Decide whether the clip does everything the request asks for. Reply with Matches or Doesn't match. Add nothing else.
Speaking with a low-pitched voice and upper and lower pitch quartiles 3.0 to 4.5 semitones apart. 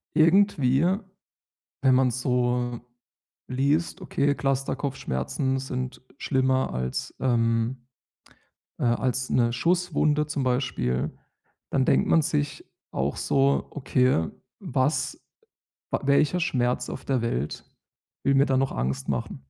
Doesn't match